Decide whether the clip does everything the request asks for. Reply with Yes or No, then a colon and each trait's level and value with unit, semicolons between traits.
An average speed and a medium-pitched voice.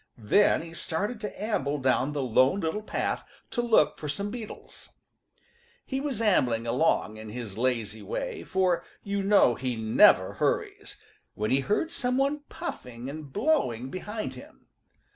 Yes: average, 155 wpm; medium, 165 Hz